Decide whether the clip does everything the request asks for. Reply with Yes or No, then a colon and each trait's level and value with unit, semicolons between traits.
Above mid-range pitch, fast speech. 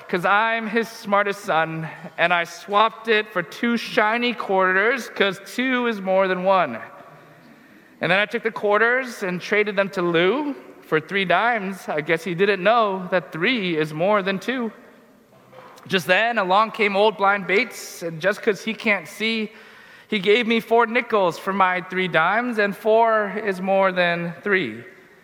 No: high, 200 Hz; average, 170 wpm